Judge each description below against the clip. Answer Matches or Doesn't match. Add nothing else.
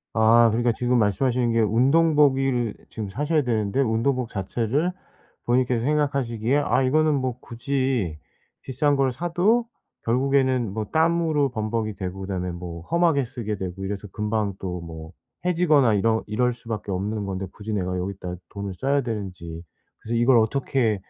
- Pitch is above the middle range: Doesn't match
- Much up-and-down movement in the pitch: Doesn't match